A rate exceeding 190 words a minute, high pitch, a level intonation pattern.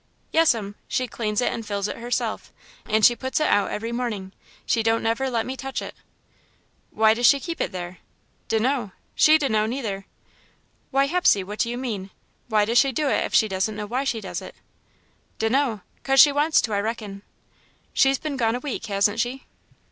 No: average, 200 wpm; high, 230 Hz; average, 4.1 semitones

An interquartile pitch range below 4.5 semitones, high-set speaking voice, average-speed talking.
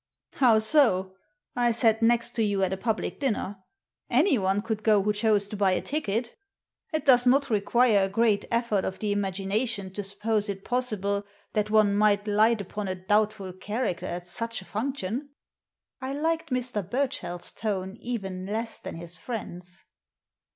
Yes: average, 3.3 semitones; high, 210 Hz; average, 165 wpm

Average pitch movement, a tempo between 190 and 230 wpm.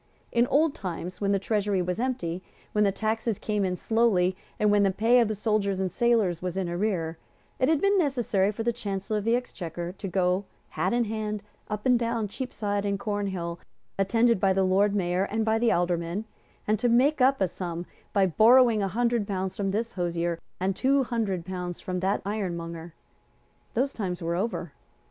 Yes: average, 3.9 semitones; average, 195 wpm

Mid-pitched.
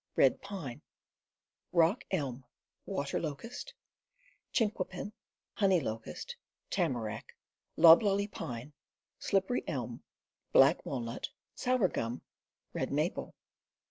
Yes: medium, 165 Hz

